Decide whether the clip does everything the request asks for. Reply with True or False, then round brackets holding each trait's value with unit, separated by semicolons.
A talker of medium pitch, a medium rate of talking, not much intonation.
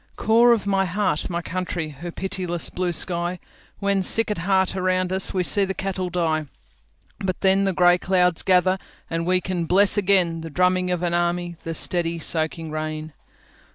True (180 Hz; 150 wpm; 2.2 semitones)